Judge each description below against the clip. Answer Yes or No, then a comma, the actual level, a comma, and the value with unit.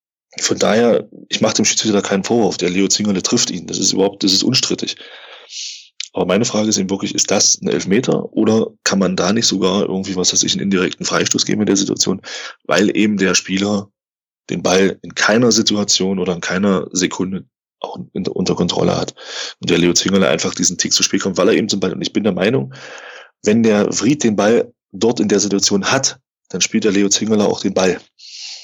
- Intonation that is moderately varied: No, narrow, 2.0 semitones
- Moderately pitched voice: No, low, 100 Hz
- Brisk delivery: Yes, fast, 215 wpm